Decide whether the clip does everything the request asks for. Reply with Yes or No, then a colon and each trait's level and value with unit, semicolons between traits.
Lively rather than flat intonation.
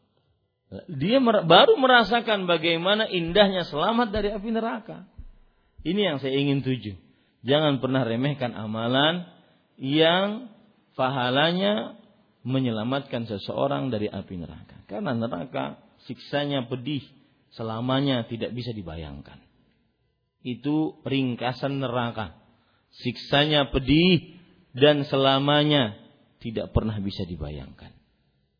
Yes: wide, 6.3 semitones